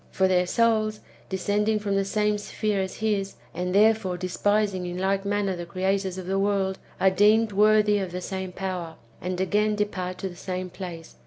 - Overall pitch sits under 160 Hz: No, high, 195 Hz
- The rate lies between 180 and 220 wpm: Yes, average, 185 wpm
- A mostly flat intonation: Yes, narrow, 2.1 semitones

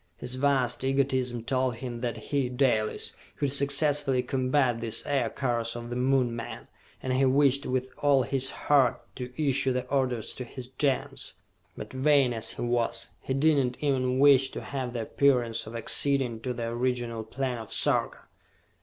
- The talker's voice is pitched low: Yes, low, 130 Hz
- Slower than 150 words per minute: No, average, 170 wpm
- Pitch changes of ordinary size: No, narrow, 2.2 semitones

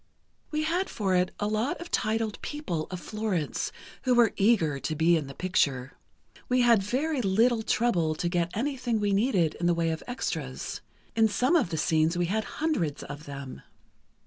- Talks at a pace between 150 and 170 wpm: No, average, 185 wpm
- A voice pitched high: Yes, high, 200 Hz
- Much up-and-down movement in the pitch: Yes, wide, 6.5 semitones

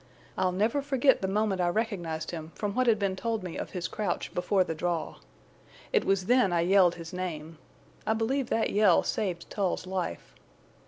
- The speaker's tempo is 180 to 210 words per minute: Yes, average, 190 wpm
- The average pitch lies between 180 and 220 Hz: Yes, high, 190 Hz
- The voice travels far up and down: No, average, 3.9 semitones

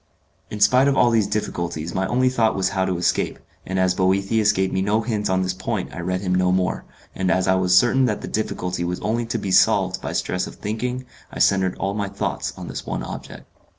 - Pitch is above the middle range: No, very low, 95 Hz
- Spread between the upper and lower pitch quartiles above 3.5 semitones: No, average, 2.9 semitones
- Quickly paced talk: Yes, fast, 235 wpm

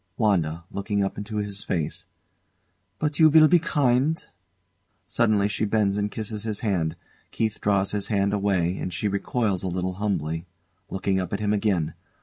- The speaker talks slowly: No, average, 165 wpm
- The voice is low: Yes, low, 100 Hz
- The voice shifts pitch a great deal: No, narrow, 2.4 semitones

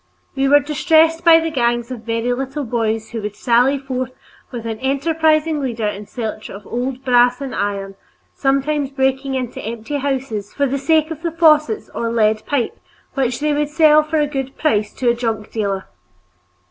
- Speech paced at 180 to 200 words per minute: Yes, average, 185 wpm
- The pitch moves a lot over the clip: No, average, 4.3 semitones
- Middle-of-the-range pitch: No, very high, 265 Hz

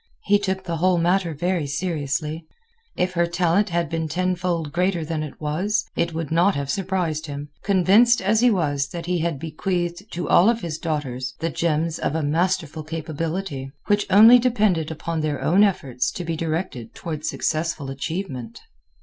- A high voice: No, medium, 170 Hz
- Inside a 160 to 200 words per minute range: Yes, average, 175 wpm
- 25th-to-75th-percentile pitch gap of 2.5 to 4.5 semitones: Yes, average, 3.3 semitones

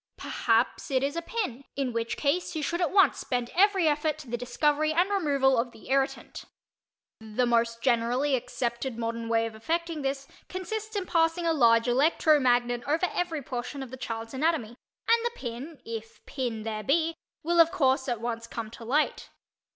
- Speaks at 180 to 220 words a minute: Yes, average, 185 wpm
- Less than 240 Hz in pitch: No, very high, 270 Hz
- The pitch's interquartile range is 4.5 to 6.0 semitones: Yes, wide, 5.6 semitones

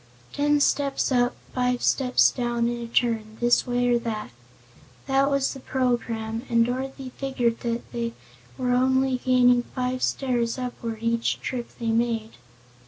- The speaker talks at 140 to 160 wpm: Yes, average, 155 wpm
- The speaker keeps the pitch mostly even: Yes, narrow, 1.7 semitones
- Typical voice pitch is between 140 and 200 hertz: No, high, 245 Hz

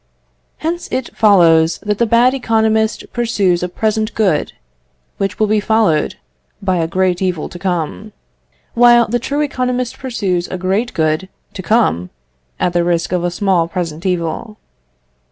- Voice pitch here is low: No, high, 195 Hz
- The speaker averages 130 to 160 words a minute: Yes, average, 155 wpm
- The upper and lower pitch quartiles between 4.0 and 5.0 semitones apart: Yes, average, 4.5 semitones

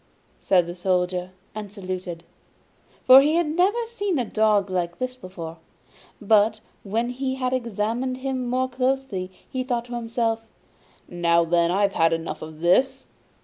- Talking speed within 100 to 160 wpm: Yes, average, 150 wpm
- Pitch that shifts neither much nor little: No, wide, 6.0 semitones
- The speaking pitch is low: No, high, 220 Hz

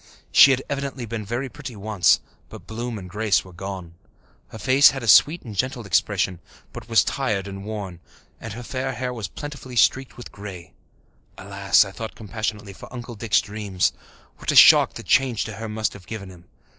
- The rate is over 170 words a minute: Yes, average, 195 wpm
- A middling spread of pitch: Yes, average, 4.0 semitones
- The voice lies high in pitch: No, low, 110 Hz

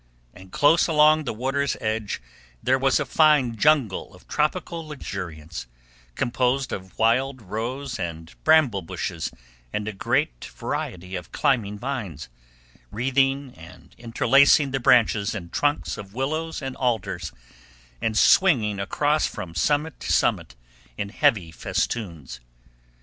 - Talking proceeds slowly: Yes, slow, 130 wpm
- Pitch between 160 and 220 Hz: No, low, 120 Hz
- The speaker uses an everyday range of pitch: No, wide, 6.8 semitones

